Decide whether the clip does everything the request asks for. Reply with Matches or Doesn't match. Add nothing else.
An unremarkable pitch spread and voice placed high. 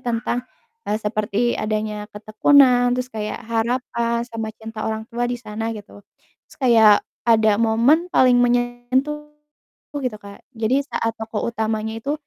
Doesn't match